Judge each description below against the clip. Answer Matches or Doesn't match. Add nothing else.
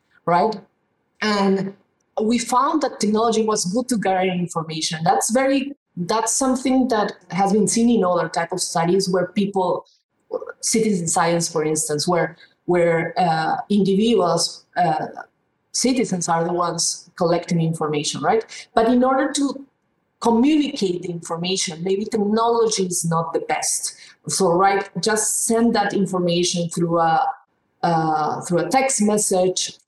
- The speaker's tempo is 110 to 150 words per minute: Matches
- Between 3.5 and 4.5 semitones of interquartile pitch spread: Doesn't match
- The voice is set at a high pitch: Matches